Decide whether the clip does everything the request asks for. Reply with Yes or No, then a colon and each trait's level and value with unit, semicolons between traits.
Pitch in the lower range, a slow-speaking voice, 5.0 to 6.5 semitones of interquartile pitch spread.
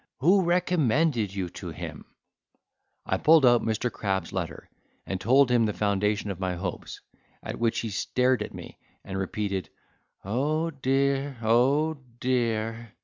No: low, 115 Hz; average, 145 wpm; wide, 5.4 semitones